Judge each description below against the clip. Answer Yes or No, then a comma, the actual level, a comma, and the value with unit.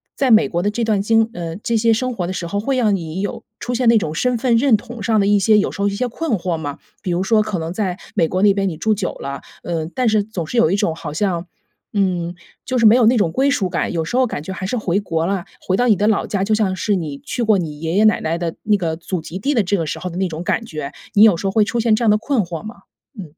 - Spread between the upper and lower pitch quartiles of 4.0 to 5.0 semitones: Yes, average, 4.4 semitones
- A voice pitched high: Yes, high, 200 Hz